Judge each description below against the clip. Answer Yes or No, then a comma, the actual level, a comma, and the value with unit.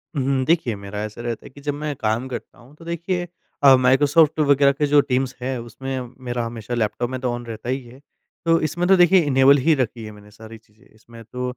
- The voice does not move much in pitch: No, average, 3.7 semitones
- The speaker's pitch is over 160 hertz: No, low, 130 Hz